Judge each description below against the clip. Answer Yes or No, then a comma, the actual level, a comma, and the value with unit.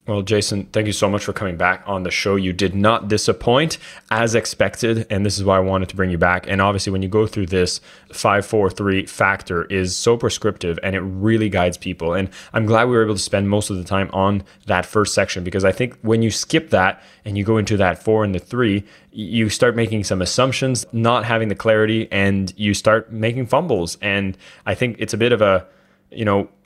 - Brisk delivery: Yes, fast, 225 wpm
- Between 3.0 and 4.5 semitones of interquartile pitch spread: No, narrow, 2.5 semitones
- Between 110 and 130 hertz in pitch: No, low, 100 Hz